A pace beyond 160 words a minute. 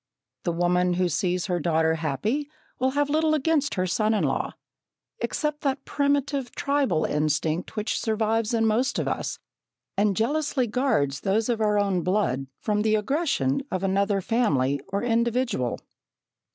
No: average, 150 wpm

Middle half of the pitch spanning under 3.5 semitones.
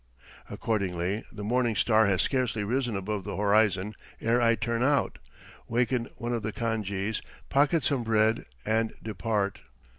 Yes: narrow, 2.4 semitones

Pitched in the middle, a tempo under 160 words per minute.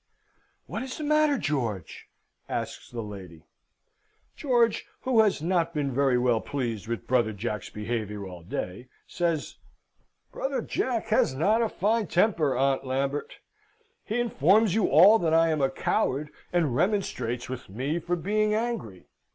Yes: medium, 150 Hz; average, 150 wpm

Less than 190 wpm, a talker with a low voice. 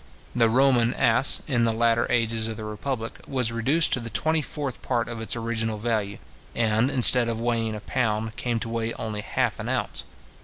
No: average, 195 wpm; low, 115 Hz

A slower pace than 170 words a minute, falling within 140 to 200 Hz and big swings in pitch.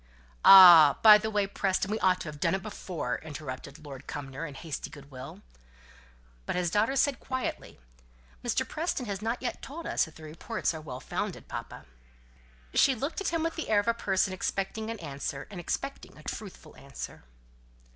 No: average, 185 wpm; high, 190 Hz; wide, 6.5 semitones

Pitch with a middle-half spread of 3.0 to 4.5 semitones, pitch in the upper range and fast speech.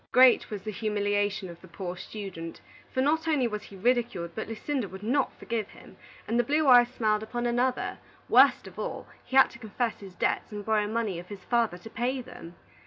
Yes: average, 3.5 semitones; high, 220 Hz; fast, 210 wpm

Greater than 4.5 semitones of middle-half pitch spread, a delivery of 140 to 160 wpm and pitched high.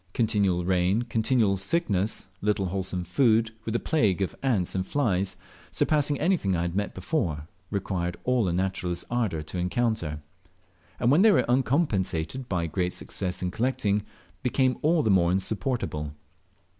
No: wide, 5.4 semitones; average, 155 wpm; low, 100 Hz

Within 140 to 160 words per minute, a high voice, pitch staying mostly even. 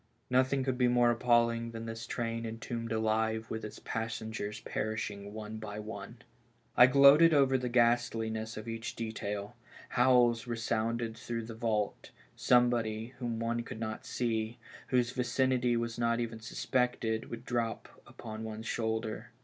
No: average, 145 wpm; low, 115 Hz; narrow, 1.6 semitones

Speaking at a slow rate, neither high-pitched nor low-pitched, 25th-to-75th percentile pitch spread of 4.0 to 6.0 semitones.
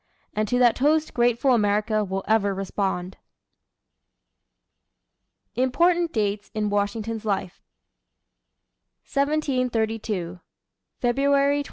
No: slow, 85 wpm; high, 225 Hz; average, 4.5 semitones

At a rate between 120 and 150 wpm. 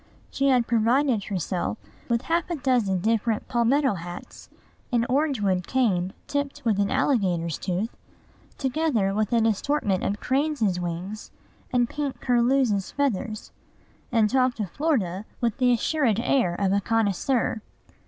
Yes: average, 140 wpm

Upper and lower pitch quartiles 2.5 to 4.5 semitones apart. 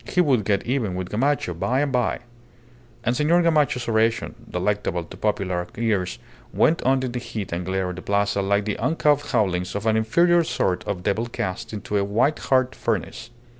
No: average, 5.0 semitones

